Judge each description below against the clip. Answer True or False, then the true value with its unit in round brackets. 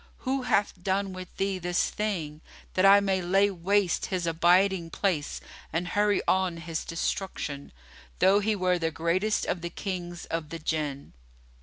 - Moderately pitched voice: True (180 Hz)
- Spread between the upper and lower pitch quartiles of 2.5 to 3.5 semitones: True (2.8 semitones)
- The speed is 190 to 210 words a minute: False (160 wpm)